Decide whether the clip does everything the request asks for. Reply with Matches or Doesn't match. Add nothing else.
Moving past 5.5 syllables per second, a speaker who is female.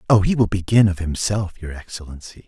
Doesn't match